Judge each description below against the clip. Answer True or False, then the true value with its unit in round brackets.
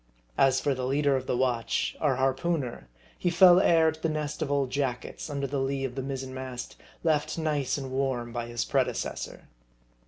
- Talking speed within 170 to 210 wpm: True (195 wpm)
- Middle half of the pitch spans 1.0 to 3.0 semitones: True (2.5 semitones)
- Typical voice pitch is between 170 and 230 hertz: False (135 Hz)